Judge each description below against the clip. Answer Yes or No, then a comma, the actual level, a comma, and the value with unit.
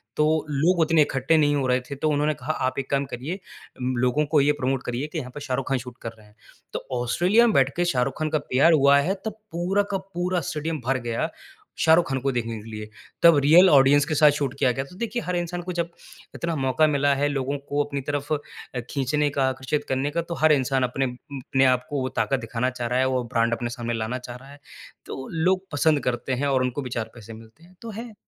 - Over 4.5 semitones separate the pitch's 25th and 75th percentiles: No, average, 3.7 semitones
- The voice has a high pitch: No, medium, 140 Hz